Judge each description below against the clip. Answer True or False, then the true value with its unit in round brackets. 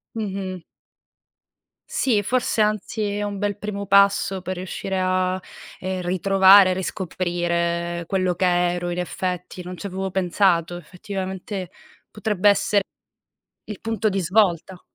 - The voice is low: False (185 Hz)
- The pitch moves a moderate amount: False (2.1 semitones)